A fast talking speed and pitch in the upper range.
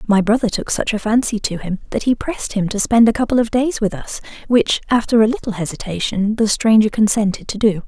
Yes: fast, 230 wpm; high, 220 Hz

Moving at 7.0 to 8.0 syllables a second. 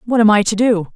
No: 6.0 syllables/s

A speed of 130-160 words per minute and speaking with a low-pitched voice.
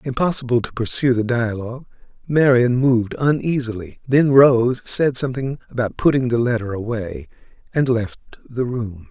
Yes: average, 140 wpm; low, 125 Hz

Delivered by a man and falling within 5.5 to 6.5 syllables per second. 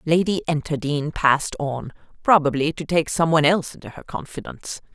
No: female; 5.7 syllables/s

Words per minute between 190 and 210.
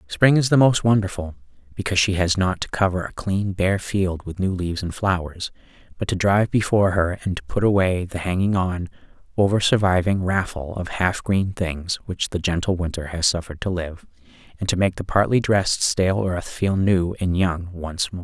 Yes: average, 200 wpm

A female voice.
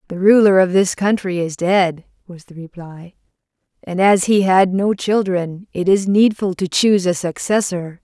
Yes: female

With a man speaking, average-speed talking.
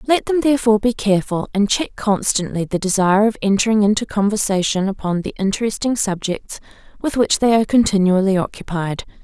No: female; average, 155 wpm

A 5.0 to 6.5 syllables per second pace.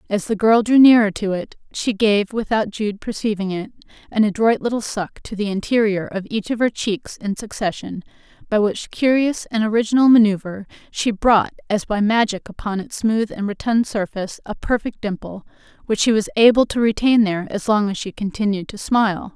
Yes: 5.3 syllables/s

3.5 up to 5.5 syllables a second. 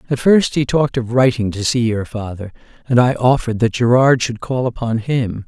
Yes: 5.3 syllables/s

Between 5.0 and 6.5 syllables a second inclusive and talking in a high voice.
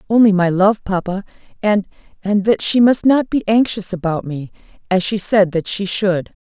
No: 4.8 syllables/s; high, 200 Hz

